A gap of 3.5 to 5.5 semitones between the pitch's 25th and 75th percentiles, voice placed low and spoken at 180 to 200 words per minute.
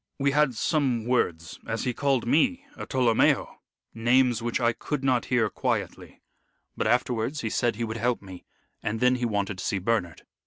No: average, 2.7 semitones; low, 120 Hz; average, 185 wpm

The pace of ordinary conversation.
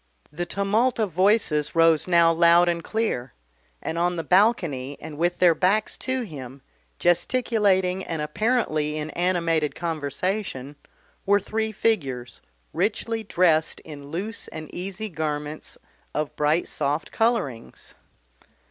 No: slow, 125 wpm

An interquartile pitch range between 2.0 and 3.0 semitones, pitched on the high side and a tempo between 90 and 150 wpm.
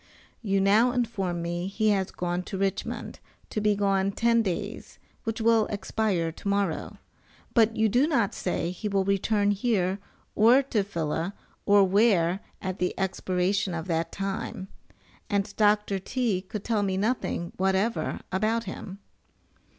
Yes: narrow, 2.6 semitones; high, 200 Hz; average, 145 wpm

